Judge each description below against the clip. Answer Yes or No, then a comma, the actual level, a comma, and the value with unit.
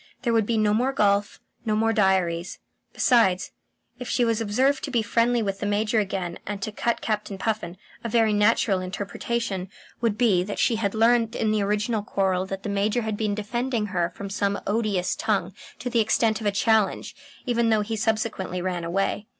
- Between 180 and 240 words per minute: Yes, average, 195 wpm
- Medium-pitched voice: No, high, 210 Hz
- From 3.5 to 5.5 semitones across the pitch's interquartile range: No, narrow, 2.6 semitones